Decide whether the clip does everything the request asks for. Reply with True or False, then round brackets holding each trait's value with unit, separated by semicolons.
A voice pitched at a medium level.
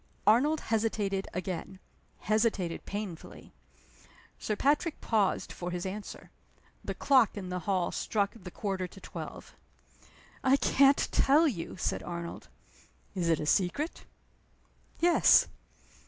False (200 Hz)